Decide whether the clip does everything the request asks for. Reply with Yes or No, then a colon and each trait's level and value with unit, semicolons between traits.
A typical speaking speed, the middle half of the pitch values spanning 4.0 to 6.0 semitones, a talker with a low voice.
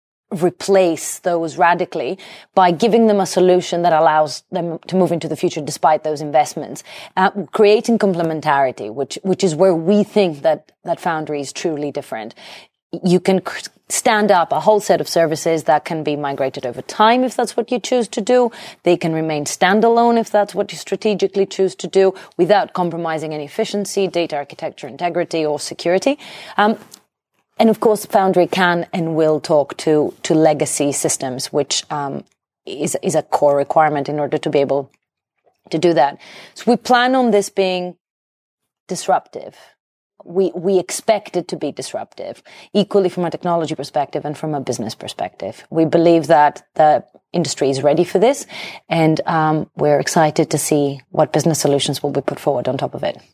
No: average, 175 wpm; average, 4.3 semitones; medium, 170 Hz